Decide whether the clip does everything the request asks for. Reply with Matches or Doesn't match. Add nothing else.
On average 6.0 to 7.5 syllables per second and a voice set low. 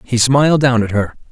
Doesn't match